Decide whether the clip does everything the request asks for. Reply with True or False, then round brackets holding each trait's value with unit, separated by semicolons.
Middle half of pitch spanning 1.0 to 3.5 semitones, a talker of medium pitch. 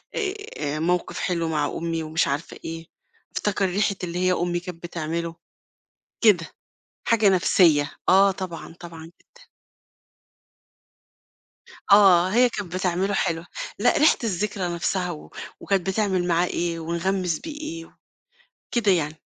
True (3.0 semitones; 180 Hz)